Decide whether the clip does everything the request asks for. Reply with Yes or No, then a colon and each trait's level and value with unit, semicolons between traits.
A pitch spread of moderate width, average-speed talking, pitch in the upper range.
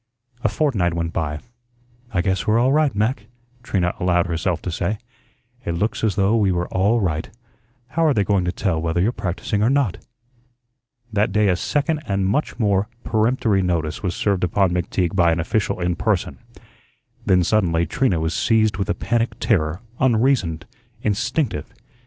No: average, 4.2 semitones; average, 170 wpm; low, 100 Hz